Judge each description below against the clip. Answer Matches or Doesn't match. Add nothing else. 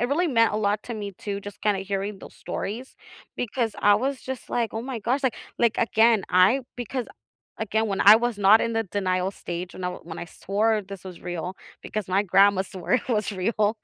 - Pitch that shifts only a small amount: Doesn't match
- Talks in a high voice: Matches